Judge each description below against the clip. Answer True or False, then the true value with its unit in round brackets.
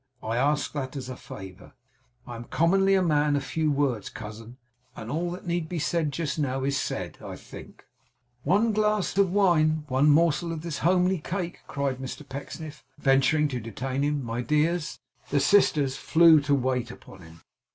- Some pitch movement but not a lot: True (4.3 semitones)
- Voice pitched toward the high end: False (150 Hz)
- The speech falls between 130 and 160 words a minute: False (185 wpm)